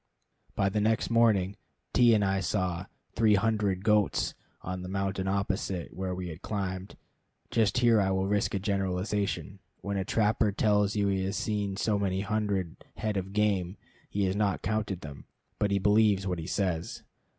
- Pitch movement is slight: Yes, narrow, 1.9 semitones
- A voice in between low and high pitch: No, low, 100 Hz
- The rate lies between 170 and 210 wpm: Yes, average, 175 wpm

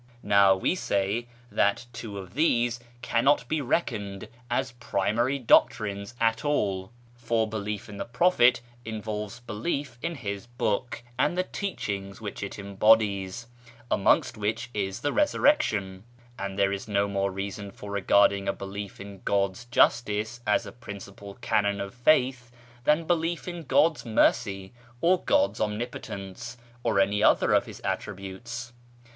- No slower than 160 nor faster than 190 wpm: No, average, 140 wpm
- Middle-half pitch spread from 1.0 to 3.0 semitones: No, average, 3.4 semitones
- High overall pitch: No, low, 110 Hz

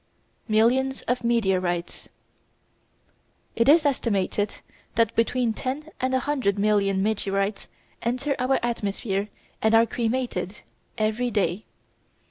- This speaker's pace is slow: Yes, slow, 105 wpm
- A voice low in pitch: No, high, 225 Hz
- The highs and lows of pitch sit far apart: No, average, 4.0 semitones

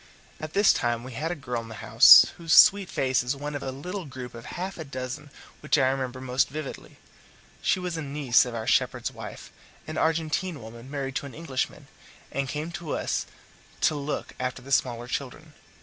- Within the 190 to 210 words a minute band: Yes, average, 200 wpm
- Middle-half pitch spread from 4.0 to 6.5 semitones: No, average, 3.6 semitones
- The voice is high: No, medium, 140 Hz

